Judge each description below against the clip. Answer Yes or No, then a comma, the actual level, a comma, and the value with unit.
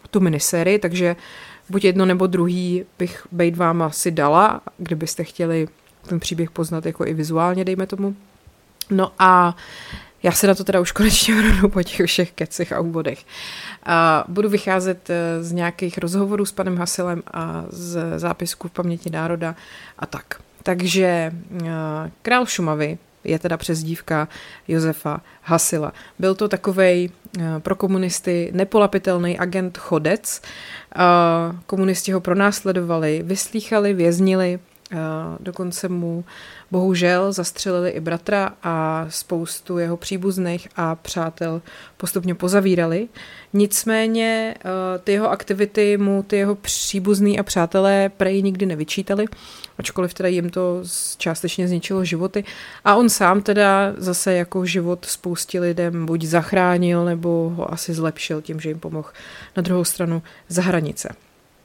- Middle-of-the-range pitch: Yes, medium, 180 Hz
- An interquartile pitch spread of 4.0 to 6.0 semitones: No, narrow, 2.4 semitones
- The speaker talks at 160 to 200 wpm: No, average, 130 wpm